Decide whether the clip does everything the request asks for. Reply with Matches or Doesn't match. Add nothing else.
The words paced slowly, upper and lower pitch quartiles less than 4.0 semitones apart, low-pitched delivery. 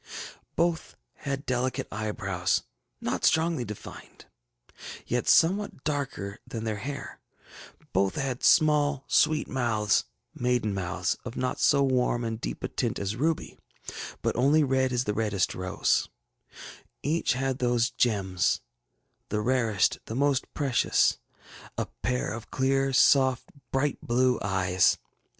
Doesn't match